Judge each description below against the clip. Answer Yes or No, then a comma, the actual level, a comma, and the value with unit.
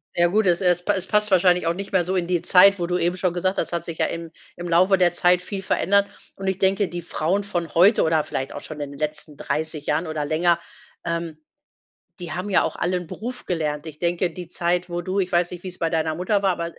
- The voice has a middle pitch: Yes, medium, 175 Hz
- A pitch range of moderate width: No, narrow, 2.1 semitones